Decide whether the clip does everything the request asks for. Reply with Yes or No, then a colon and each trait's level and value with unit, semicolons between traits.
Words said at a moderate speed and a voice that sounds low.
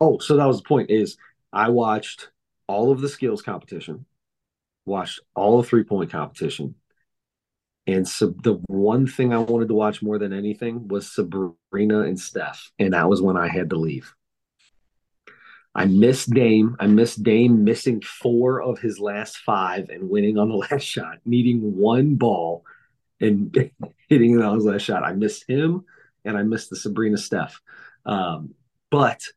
Yes: average, 170 wpm; low, 110 Hz